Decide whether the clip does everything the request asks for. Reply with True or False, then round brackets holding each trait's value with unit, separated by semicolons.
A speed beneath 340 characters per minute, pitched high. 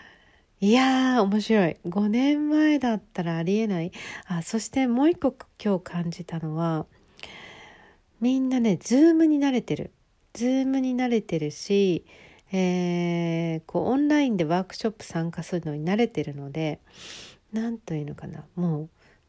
True (290 characters per minute; 195 Hz)